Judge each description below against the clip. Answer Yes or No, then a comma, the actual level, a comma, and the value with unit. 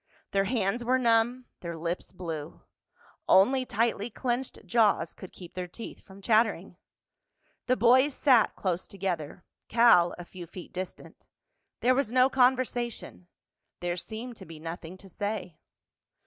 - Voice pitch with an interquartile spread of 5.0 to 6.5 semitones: Yes, average, 5.3 semitones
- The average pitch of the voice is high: Yes, high, 205 Hz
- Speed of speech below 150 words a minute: Yes, slow, 135 wpm